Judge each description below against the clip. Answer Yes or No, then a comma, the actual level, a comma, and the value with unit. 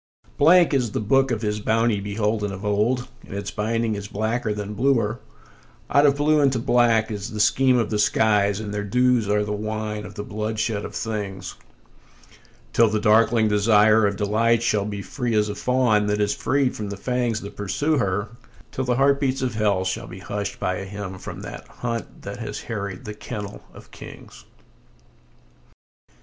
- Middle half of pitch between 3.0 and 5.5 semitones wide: No, narrow, 2.5 semitones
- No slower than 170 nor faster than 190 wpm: Yes, average, 185 wpm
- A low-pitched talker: Yes, low, 110 Hz